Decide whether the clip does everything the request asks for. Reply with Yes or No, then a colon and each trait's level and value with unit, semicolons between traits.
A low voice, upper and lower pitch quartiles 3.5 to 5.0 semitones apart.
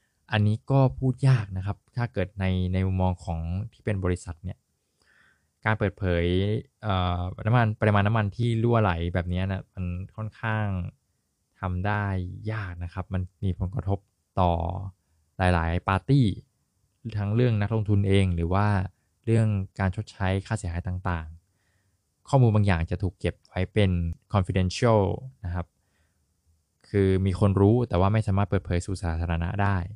No: very low, 95 Hz; average, 3.0 semitones